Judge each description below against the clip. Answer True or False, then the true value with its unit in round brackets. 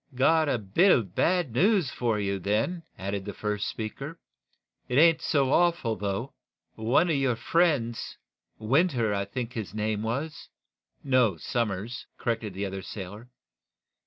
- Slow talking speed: False (155 wpm)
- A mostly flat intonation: False (5.5 semitones)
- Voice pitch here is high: False (115 Hz)